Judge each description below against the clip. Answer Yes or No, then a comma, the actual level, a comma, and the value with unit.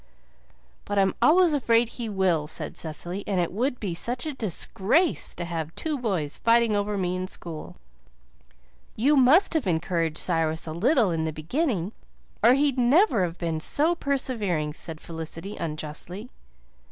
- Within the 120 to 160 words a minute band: Yes, average, 155 wpm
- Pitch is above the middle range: Yes, high, 195 Hz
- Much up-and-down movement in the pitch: Yes, wide, 7.1 semitones